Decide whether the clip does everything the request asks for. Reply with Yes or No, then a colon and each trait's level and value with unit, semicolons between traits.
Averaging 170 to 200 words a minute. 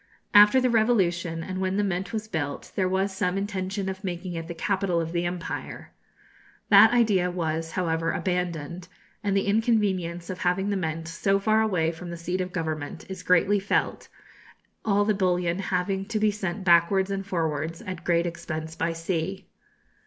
Yes: average, 175 wpm